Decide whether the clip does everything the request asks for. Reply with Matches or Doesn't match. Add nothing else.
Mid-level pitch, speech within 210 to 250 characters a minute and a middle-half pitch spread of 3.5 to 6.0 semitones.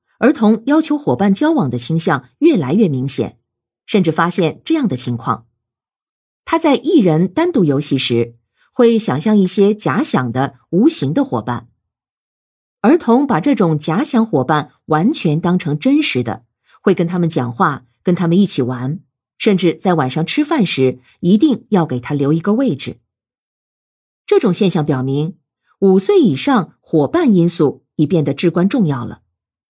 Doesn't match